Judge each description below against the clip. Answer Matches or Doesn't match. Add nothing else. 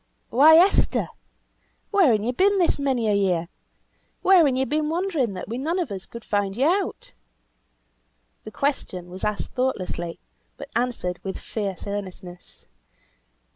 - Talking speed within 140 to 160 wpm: Matches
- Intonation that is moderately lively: Doesn't match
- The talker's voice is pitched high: Matches